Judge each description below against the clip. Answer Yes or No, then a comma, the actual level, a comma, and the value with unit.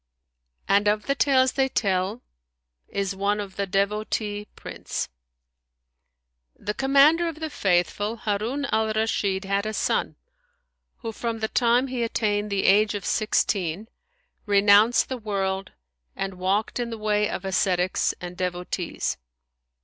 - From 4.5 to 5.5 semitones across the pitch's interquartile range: No, average, 2.8 semitones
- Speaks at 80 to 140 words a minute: Yes, slow, 135 wpm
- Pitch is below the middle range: No, high, 210 Hz